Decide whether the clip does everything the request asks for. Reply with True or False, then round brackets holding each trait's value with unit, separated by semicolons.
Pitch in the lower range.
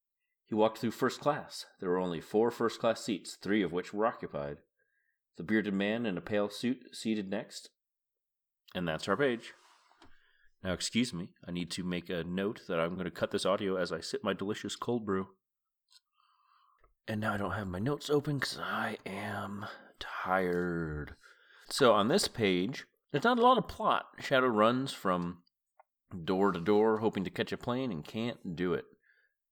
True (105 Hz)